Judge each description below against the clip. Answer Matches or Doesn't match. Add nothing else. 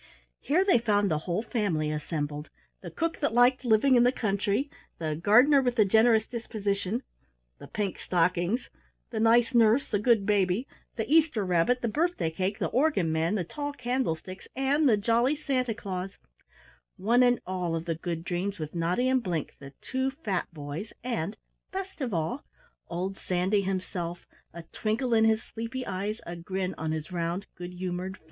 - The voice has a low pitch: Doesn't match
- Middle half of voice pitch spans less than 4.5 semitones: Doesn't match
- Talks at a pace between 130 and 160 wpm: Doesn't match